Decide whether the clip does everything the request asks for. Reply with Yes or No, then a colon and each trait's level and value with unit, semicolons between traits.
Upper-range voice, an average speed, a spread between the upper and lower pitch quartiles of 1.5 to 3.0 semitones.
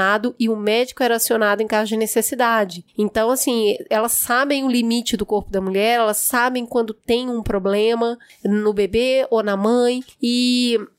Yes: high, 230 Hz; average, 170 wpm; narrow, 2.4 semitones